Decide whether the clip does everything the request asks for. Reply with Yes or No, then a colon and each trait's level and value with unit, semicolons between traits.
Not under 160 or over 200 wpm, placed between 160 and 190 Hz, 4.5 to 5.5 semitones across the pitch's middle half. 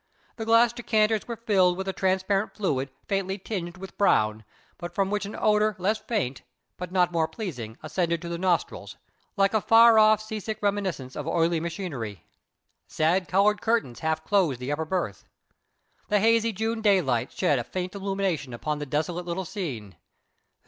Yes: average, 170 wpm; medium, 185 Hz; average, 4.8 semitones